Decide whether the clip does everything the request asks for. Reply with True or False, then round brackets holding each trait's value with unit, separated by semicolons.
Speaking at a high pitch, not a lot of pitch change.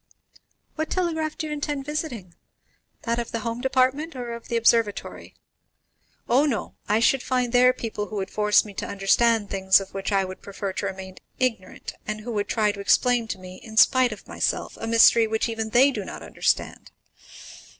False (230 Hz; 3.8 semitones)